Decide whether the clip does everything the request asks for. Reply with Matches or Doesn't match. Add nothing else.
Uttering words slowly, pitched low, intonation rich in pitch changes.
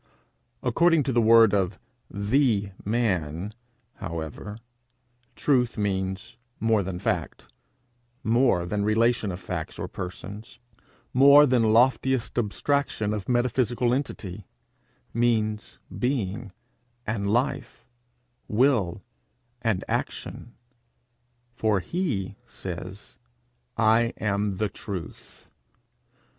Doesn't match